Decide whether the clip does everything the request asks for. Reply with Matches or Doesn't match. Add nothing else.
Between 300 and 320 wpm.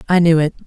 Doesn't match